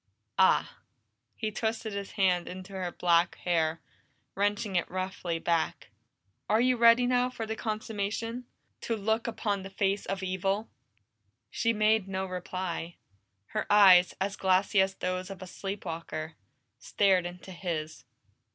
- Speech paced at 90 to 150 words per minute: Yes, average, 140 wpm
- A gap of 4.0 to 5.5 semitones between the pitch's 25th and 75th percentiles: No, average, 2.9 semitones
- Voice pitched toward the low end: No, high, 195 Hz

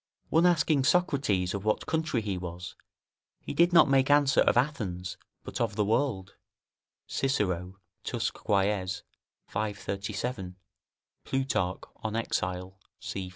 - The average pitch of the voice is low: Yes, low, 105 Hz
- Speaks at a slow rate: Yes, slow, 125 wpm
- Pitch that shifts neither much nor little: No, wide, 6.6 semitones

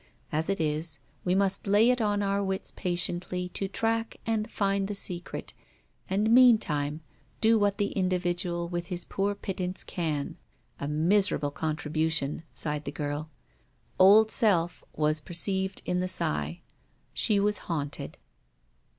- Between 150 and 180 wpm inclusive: No, average, 140 wpm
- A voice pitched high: No, medium, 180 Hz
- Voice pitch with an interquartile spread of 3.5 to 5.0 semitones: Yes, average, 4.3 semitones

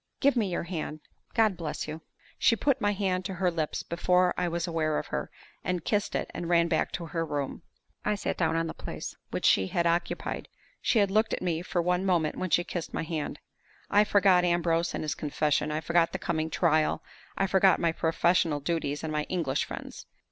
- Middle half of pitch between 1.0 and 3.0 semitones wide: Yes, narrow, 2.6 semitones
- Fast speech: Yes, fast, 215 wpm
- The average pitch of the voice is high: No, medium, 170 Hz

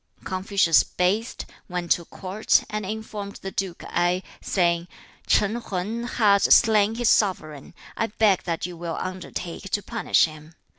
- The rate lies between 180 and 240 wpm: No, average, 150 wpm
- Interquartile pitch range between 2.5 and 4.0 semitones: Yes, average, 3.4 semitones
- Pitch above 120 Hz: Yes, high, 190 Hz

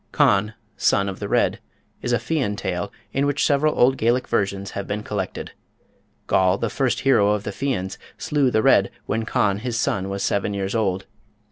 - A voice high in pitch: No, low, 105 Hz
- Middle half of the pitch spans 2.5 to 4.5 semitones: Yes, average, 4.2 semitones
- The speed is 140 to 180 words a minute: No, average, 190 wpm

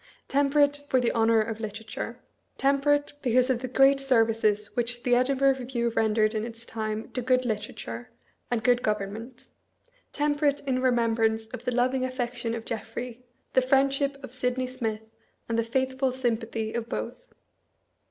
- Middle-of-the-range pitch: No, high, 245 Hz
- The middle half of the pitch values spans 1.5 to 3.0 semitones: Yes, narrow, 2.6 semitones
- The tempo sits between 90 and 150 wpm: No, average, 160 wpm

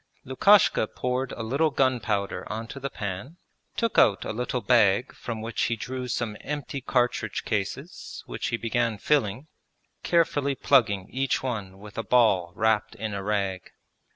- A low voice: Yes, low, 115 Hz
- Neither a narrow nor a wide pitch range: Yes, average, 4.1 semitones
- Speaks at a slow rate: No, average, 155 wpm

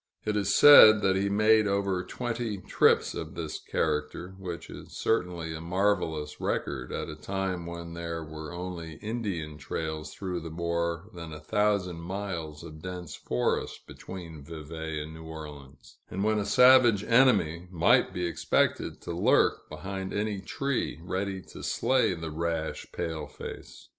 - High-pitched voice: No, very low, 90 Hz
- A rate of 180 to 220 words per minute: No, average, 155 wpm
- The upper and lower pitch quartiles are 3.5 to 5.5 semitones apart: Yes, average, 3.8 semitones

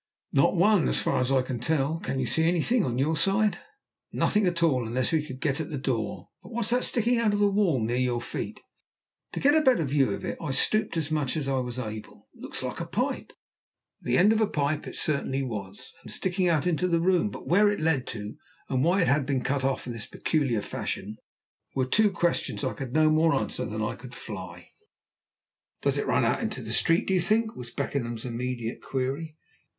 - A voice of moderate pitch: Yes, medium, 150 Hz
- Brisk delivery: Yes, fast, 225 wpm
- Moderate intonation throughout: No, wide, 5.9 semitones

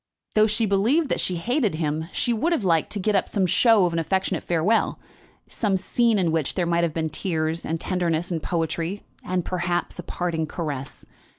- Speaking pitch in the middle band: Yes, medium, 180 Hz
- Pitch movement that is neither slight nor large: Yes, average, 4.0 semitones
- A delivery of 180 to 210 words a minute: Yes, average, 200 wpm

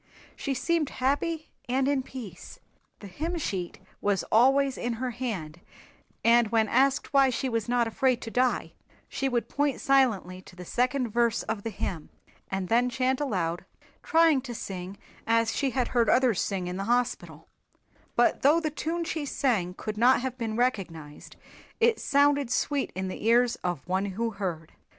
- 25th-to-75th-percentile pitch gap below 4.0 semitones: No, average, 5.2 semitones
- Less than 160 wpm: No, average, 175 wpm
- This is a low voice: No, high, 240 Hz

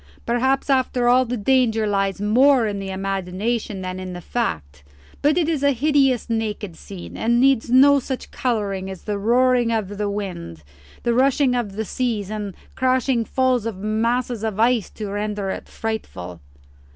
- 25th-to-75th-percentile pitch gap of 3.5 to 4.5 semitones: Yes, average, 4.2 semitones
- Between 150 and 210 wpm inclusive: Yes, average, 165 wpm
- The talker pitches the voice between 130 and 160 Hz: No, high, 225 Hz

